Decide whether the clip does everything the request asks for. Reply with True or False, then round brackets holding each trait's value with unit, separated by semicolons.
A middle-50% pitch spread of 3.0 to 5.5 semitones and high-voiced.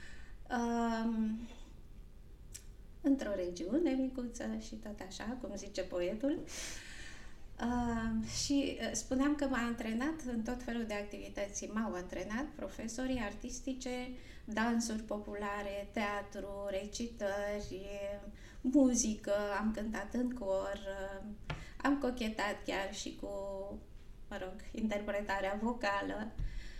True (3.9 semitones; 220 Hz)